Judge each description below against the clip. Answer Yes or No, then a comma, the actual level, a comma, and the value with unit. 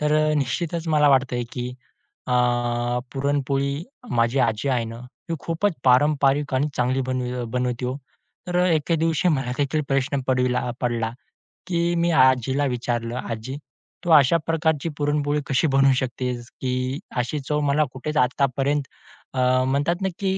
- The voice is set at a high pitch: No, low, 135 Hz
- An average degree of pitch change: Yes, average, 3.2 semitones